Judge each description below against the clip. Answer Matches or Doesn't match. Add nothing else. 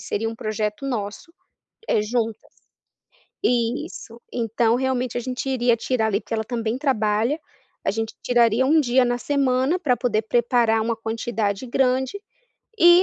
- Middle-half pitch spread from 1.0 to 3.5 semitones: Matches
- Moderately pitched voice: Doesn't match